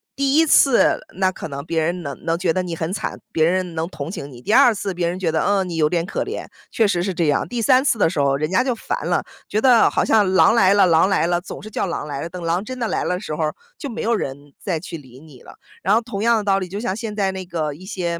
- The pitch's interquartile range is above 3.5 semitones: Yes, average, 4.4 semitones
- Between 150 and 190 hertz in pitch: Yes, medium, 185 Hz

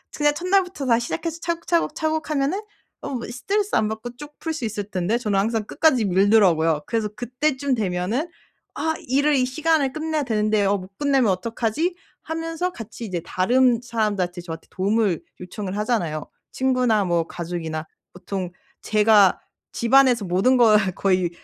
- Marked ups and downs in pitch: Yes, wide, 6.5 semitones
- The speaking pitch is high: Yes, high, 230 Hz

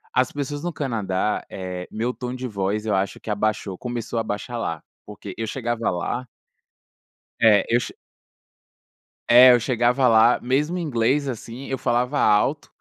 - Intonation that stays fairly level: No, average, 3.4 semitones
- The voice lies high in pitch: No, low, 120 Hz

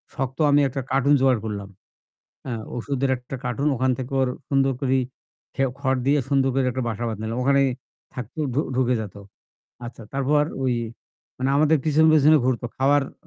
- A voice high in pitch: No, low, 135 Hz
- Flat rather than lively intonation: Yes, narrow, 2.0 semitones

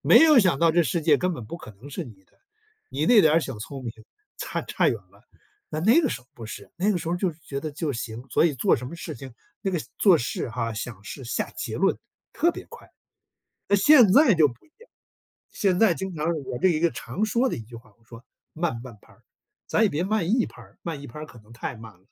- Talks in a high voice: No, medium, 155 Hz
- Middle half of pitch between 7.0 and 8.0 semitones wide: Yes, wide, 7.6 semitones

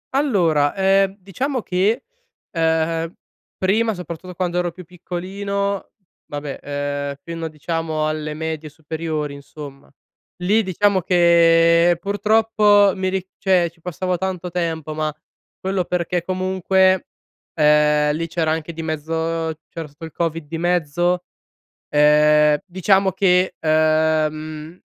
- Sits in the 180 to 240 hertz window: No, medium, 170 Hz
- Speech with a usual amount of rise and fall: Yes, average, 3.2 semitones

